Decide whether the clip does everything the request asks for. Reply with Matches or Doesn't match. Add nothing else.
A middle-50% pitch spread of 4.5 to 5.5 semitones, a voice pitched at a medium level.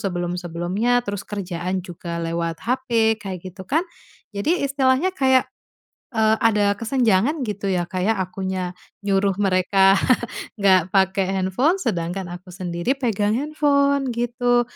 Doesn't match